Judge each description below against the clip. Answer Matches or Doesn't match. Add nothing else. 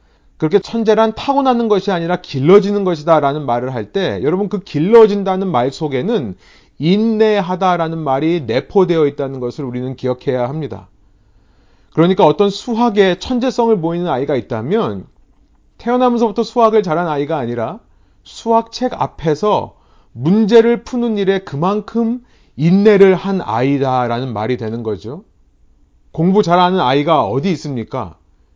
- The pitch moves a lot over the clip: Matches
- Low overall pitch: Doesn't match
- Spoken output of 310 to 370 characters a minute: Matches